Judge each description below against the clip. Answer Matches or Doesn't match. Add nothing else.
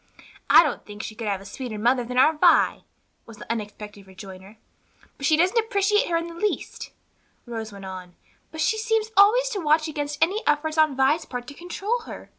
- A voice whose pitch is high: Matches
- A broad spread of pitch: Matches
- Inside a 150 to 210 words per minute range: Matches